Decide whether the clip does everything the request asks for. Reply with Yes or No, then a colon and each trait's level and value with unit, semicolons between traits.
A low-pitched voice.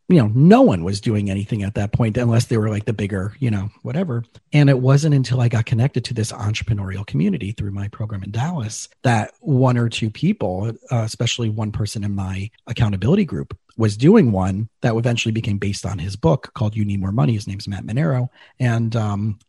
Yes: low, 115 Hz